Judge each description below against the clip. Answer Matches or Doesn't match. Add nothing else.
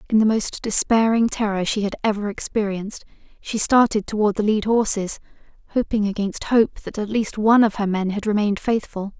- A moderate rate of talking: Matches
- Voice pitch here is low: Doesn't match